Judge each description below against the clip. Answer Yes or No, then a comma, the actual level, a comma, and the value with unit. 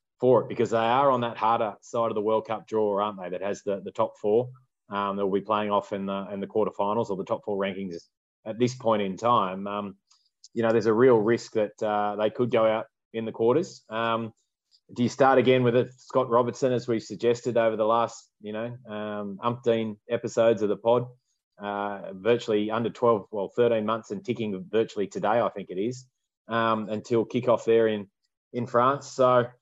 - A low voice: Yes, low, 115 Hz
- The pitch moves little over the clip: Yes, narrow, 2.3 semitones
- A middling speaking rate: No, fast, 210 wpm